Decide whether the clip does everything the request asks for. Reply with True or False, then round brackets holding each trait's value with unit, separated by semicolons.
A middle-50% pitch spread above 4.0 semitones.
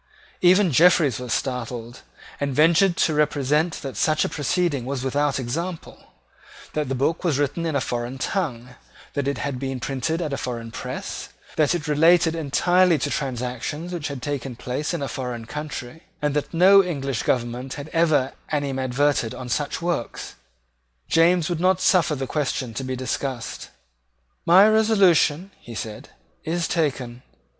True (4.5 semitones)